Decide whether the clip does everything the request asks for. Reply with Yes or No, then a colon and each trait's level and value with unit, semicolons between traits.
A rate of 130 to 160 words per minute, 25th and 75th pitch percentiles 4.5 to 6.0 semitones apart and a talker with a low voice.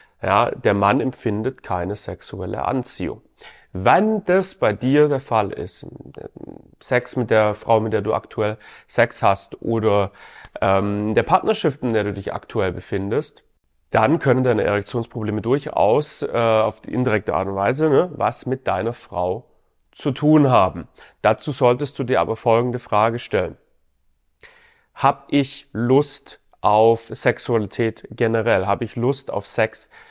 No: average, 140 wpm; average, 3.9 semitones; low, 115 Hz